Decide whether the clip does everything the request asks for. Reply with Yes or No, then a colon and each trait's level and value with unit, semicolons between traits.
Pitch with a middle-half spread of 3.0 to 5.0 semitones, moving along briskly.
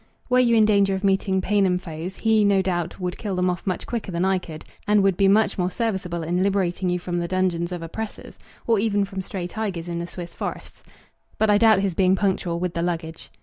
No: narrow, 2.4 semitones; fast, 235 wpm